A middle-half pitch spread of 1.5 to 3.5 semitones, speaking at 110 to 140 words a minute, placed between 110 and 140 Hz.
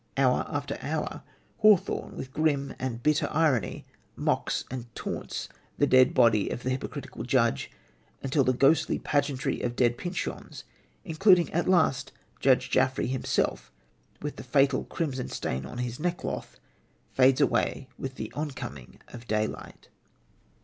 Yes: average, 3.2 semitones; slow, 135 wpm; low, 135 Hz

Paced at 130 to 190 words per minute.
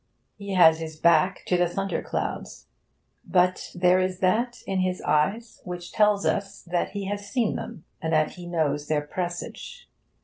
Yes: average, 165 wpm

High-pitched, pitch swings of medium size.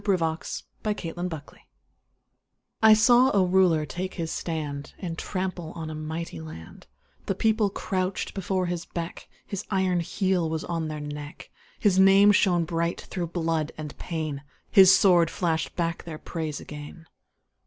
No: medium, 170 Hz; average, 3.0 semitones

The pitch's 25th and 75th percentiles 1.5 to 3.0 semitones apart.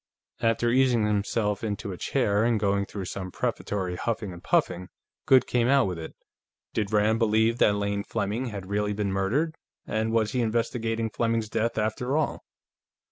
Yes: narrow, 2.5 semitones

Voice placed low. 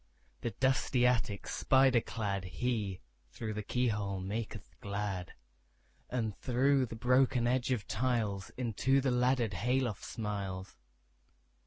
Yes: low, 115 Hz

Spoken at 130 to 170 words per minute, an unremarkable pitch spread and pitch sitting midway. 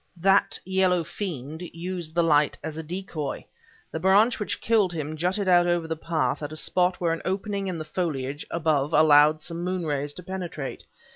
No: average, 190 wpm; average, 3.1 semitones; medium, 170 Hz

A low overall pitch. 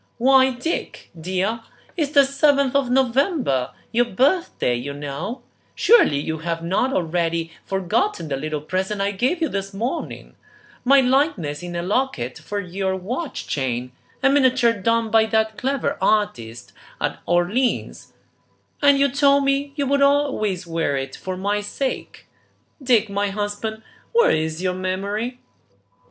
No: high, 210 Hz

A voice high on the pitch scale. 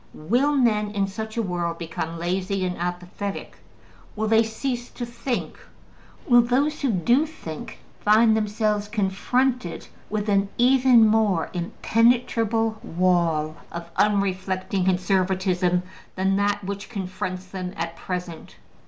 Yes: high, 200 Hz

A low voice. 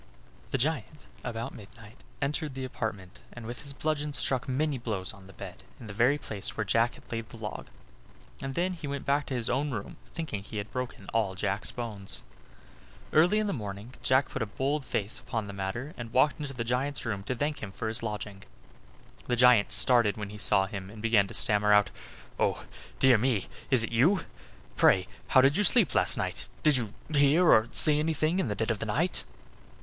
Yes: low, 120 Hz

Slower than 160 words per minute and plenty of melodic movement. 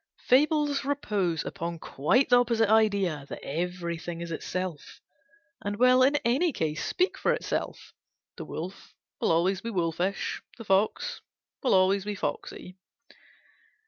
Yes: slow, 135 wpm; wide, 6.2 semitones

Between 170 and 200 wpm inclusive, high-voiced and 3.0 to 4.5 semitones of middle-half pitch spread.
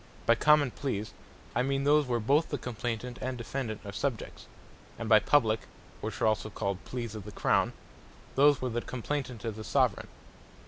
No: average, 180 wpm; low, 120 Hz; average, 3.9 semitones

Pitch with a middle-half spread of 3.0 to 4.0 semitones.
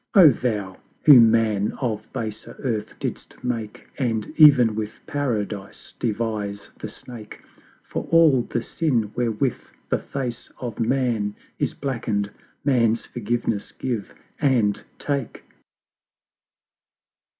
Yes: average, 3.4 semitones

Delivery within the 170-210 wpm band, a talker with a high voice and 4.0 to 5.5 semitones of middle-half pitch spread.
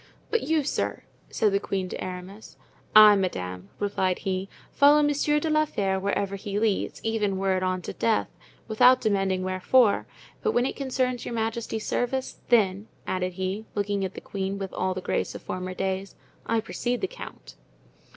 Yes: average, 180 wpm; high, 200 Hz; average, 4.3 semitones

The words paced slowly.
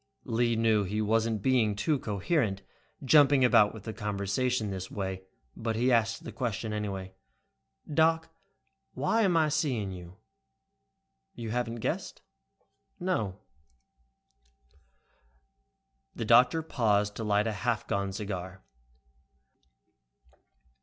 Yes: slow, 110 wpm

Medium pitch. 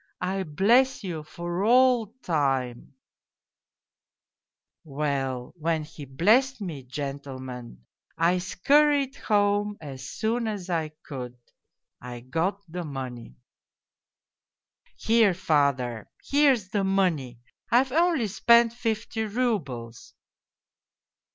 Yes: medium, 175 Hz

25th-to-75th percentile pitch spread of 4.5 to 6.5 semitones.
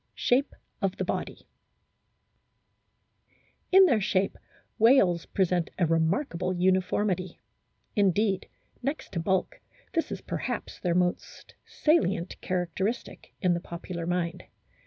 No: average, 3.3 semitones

